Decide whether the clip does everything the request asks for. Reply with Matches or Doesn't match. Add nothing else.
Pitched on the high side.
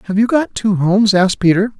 Matches